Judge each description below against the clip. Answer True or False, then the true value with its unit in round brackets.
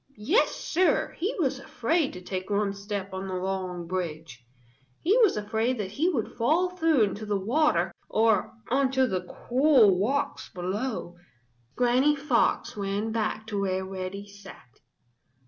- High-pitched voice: True (210 Hz)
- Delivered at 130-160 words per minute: True (145 wpm)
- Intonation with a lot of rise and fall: True (5.9 semitones)